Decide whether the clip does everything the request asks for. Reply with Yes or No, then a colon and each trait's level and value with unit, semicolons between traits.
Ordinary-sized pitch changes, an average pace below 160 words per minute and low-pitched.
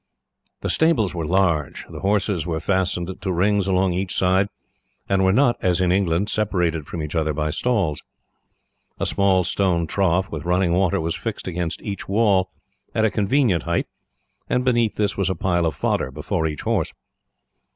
No: average, 3.0 semitones; average, 175 wpm; very low, 95 Hz